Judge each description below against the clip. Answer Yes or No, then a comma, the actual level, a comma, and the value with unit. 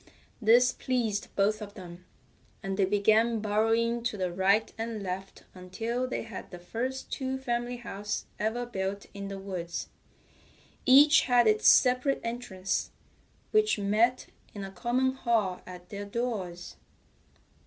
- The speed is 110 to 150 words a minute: Yes, average, 140 wpm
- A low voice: No, high, 215 Hz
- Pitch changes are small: No, average, 3.8 semitones